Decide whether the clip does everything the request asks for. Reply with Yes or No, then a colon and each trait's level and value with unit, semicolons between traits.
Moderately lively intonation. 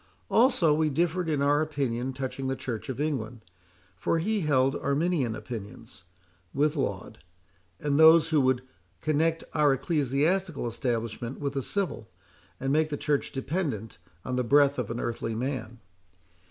Yes: average, 4.0 semitones